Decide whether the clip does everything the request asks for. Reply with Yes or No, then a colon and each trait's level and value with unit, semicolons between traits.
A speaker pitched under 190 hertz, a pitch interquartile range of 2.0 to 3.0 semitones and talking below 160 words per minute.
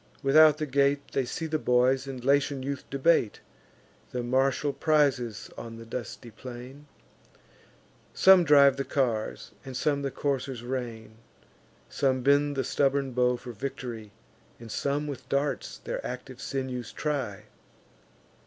Yes: low, 135 Hz; narrow, 2.4 semitones; slow, 135 wpm